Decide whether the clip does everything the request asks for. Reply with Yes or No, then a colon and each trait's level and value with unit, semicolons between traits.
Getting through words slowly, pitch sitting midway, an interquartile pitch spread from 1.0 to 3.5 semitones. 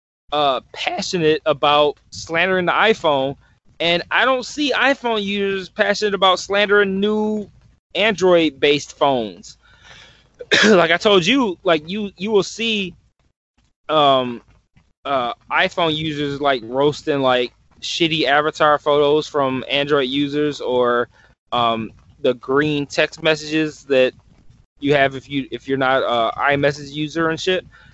No: slow, 130 wpm; medium, 155 Hz; wide, 5.5 semitones